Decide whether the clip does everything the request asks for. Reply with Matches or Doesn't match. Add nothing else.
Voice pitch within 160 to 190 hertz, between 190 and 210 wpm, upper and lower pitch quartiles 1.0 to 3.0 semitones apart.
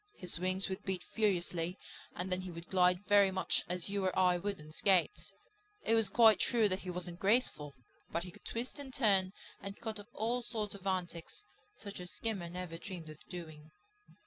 Matches